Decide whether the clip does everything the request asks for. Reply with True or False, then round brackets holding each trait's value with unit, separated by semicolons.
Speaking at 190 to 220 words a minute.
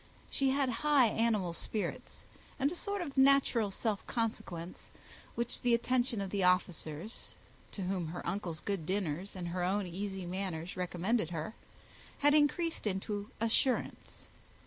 False (145 wpm)